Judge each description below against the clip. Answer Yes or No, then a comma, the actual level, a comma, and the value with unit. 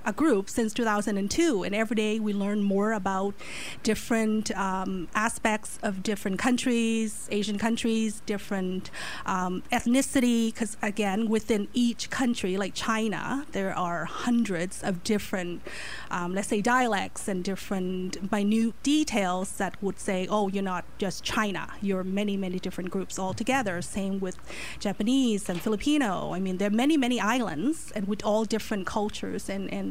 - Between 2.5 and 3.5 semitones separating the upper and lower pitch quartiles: Yes, average, 2.9 semitones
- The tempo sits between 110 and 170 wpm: Yes, average, 155 wpm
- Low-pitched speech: No, high, 210 Hz